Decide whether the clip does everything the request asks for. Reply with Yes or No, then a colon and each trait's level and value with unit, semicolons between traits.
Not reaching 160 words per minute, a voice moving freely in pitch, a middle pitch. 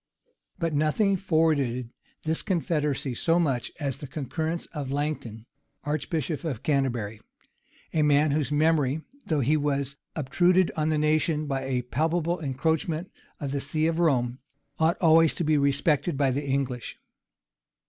No: average, 145 wpm; average, 2.9 semitones; medium, 150 Hz